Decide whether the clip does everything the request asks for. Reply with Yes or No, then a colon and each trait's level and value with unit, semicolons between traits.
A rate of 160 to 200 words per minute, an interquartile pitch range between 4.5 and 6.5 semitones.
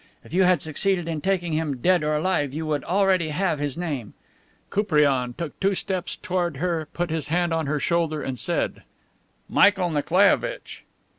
No: average, 170 wpm; average, 3.6 semitones